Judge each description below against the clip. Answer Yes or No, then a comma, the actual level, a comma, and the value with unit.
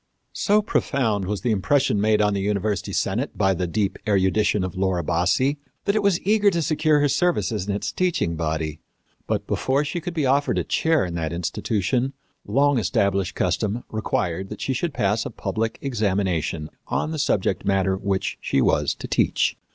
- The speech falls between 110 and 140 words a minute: No, average, 180 wpm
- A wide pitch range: Yes, wide, 6.9 semitones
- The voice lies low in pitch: Yes, low, 105 Hz